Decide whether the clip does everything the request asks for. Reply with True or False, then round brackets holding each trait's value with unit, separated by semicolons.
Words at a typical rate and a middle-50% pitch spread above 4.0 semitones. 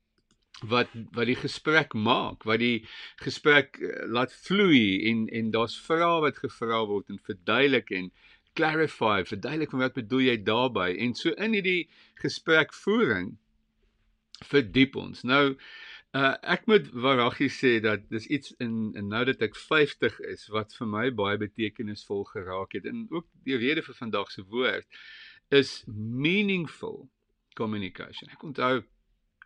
True (145 wpm; 4.7 semitones)